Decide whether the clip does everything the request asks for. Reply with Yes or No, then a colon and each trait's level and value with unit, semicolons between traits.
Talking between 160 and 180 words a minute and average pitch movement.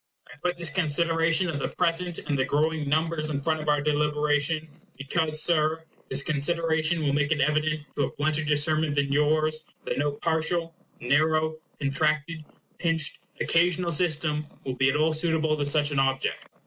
No: average, 175 wpm; narrow, 1.8 semitones